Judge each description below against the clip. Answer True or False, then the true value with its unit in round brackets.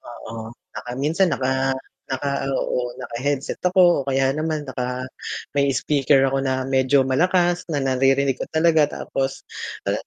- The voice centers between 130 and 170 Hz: True (135 Hz)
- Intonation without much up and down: True (2.1 semitones)